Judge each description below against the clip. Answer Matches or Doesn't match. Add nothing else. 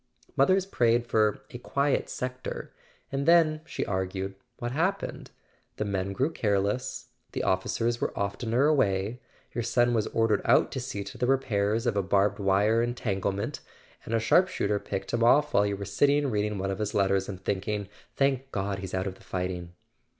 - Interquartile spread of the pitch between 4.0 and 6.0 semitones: Matches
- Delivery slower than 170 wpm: Doesn't match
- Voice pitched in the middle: Doesn't match